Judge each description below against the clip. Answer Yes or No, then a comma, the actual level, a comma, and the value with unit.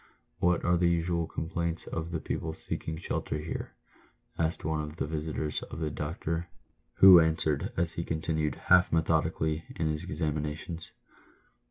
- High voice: No, very low, 80 Hz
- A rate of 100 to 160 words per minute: Yes, average, 155 wpm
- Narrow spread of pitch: Yes, narrow, 1.5 semitones